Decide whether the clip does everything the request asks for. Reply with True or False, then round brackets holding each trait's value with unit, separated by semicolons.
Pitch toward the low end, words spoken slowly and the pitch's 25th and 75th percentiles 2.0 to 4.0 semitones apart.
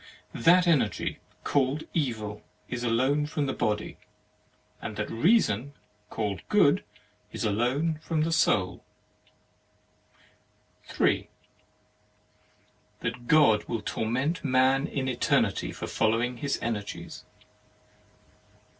False (130 Hz; 100 wpm; 4.8 semitones)